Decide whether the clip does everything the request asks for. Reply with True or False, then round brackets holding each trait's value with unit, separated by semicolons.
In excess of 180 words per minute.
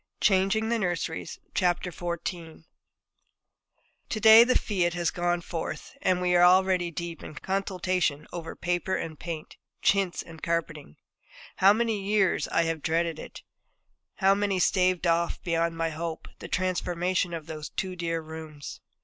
False (145 wpm)